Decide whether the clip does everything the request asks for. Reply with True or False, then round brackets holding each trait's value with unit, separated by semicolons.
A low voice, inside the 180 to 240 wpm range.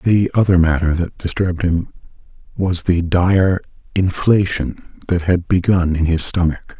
False (90 Hz; 140 wpm)